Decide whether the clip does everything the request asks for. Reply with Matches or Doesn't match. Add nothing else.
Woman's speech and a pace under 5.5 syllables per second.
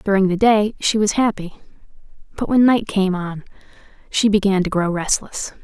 Matches